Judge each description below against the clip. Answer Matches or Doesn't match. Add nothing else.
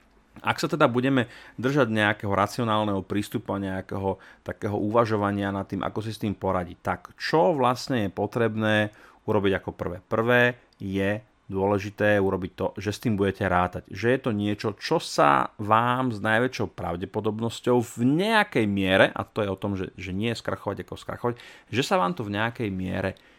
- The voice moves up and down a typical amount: Matches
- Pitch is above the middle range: Doesn't match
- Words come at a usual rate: Doesn't match